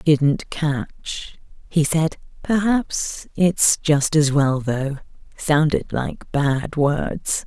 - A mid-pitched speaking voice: Yes, medium, 150 Hz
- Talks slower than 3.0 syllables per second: Yes, 2.5 syllables/s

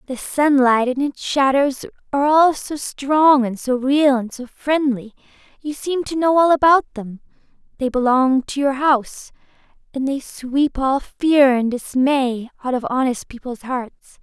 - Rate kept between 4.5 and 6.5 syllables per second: No, 4.1 syllables/s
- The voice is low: No, very high, 270 Hz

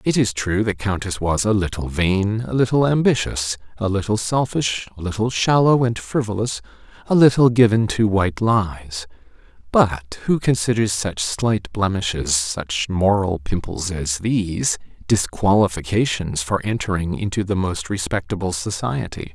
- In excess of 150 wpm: No, slow, 135 wpm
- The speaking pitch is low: Yes, low, 100 Hz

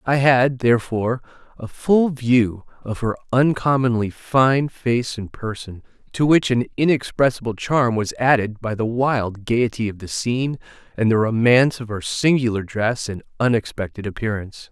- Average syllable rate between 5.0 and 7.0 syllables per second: No, 4.7 syllables/s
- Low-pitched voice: Yes, low, 120 Hz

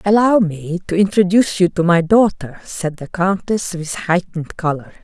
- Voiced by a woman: Yes, female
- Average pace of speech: Yes, average, 165 wpm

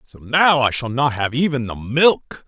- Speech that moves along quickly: Yes, fast, 220 wpm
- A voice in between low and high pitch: No, low, 130 Hz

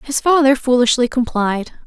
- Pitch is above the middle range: Yes, very high, 255 Hz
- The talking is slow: Yes, slow, 130 wpm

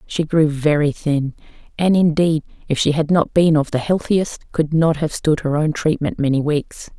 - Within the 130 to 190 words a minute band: No, fast, 205 wpm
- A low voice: No, medium, 155 Hz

